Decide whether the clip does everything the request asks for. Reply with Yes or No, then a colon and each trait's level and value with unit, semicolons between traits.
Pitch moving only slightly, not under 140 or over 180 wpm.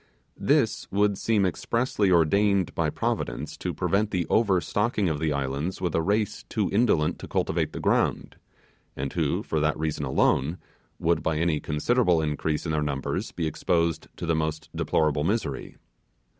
No: average, 4.8 semitones; average, 160 wpm